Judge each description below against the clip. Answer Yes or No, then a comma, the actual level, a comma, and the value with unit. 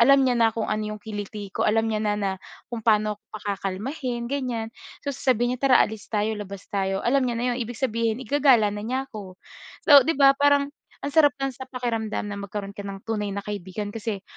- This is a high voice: Yes, high, 225 Hz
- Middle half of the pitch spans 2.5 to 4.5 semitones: Yes, average, 3.7 semitones